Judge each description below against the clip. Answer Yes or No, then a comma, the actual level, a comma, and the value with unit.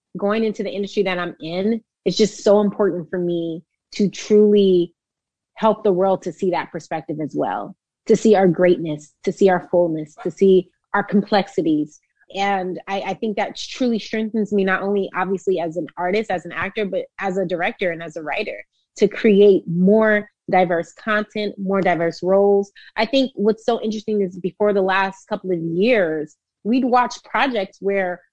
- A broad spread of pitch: No, average, 2.9 semitones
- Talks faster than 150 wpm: Yes, average, 180 wpm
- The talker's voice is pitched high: Yes, high, 195 Hz